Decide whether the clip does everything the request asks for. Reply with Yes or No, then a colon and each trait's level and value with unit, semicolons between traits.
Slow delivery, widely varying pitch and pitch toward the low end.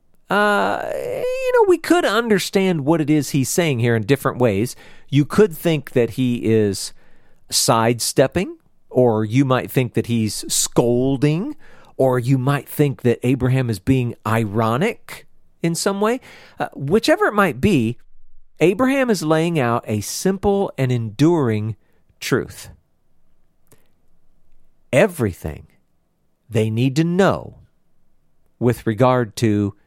Yes: slow, 125 wpm; wide, 6.9 semitones; low, 130 Hz